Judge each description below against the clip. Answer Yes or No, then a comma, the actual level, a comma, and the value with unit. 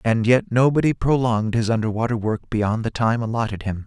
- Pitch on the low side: Yes, low, 115 Hz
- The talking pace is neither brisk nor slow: Yes, average, 185 wpm